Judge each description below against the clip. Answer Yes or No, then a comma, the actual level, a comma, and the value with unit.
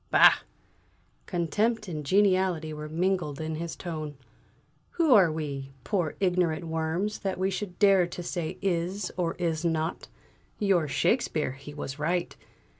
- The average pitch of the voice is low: No, medium, 170 Hz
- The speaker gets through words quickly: No, average, 140 wpm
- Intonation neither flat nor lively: Yes, average, 3.3 semitones